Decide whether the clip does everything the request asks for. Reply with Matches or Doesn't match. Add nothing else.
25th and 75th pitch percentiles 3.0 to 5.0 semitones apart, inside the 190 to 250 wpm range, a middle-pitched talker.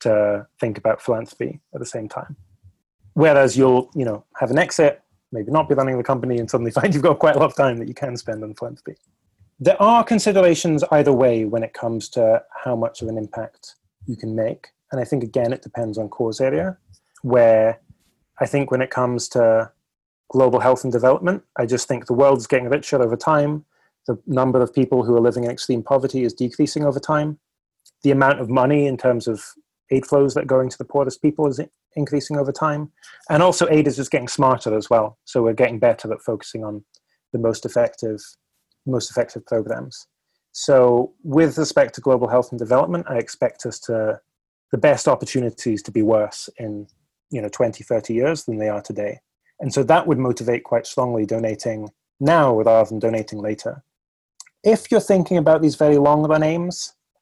Doesn't match